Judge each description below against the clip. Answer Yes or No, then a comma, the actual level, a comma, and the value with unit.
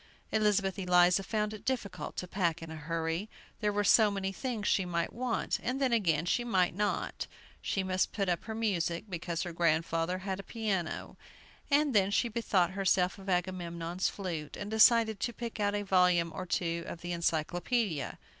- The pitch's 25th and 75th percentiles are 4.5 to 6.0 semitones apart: No, average, 3.6 semitones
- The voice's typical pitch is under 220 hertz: Yes, high, 190 Hz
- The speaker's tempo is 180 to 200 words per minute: Yes, average, 185 wpm